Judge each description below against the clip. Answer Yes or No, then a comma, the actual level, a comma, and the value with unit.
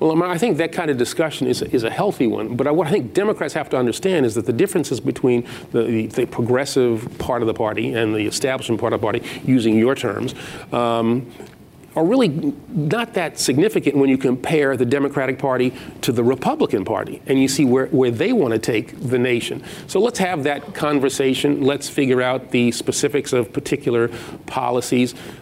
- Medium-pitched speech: No, low, 130 Hz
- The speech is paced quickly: No, average, 195 wpm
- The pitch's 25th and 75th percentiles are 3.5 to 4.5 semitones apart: No, average, 3.0 semitones